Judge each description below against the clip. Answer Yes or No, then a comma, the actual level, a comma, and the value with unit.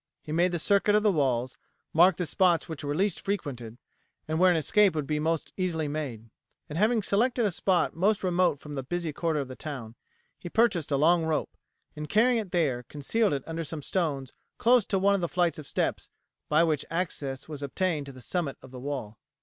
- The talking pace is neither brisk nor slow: No, fast, 215 wpm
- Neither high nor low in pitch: Yes, medium, 160 Hz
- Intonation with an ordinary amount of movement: Yes, average, 4.5 semitones